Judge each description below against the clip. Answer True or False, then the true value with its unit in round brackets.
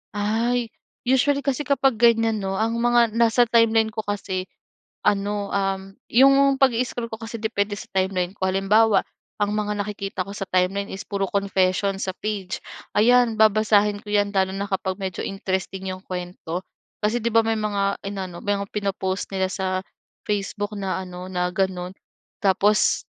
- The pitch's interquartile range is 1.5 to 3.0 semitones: True (2.7 semitones)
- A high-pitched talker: True (205 Hz)